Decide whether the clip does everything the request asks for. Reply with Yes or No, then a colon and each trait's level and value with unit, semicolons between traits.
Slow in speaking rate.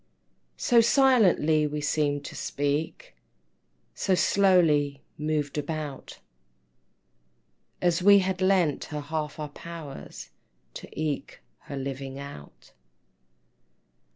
Yes: slow, 95 wpm